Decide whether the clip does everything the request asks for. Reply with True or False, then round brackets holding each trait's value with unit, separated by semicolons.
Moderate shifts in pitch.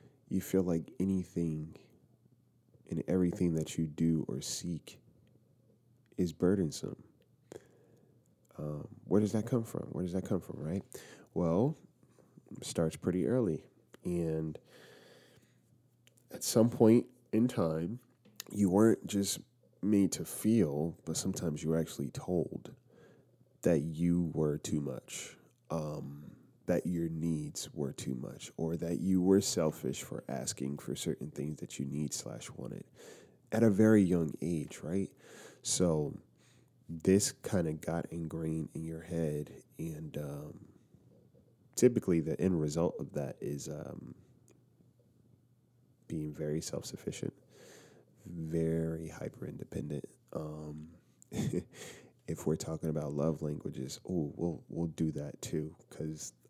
True (3.9 semitones)